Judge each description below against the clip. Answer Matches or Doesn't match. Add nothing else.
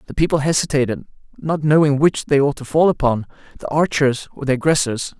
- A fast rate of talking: Doesn't match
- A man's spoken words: Matches